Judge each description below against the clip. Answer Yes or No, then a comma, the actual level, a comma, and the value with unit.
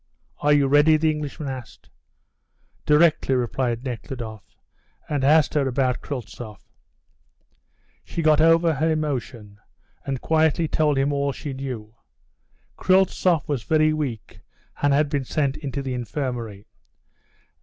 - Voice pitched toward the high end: No, medium, 140 Hz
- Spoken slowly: Yes, slow, 125 wpm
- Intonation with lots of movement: No, average, 3.4 semitones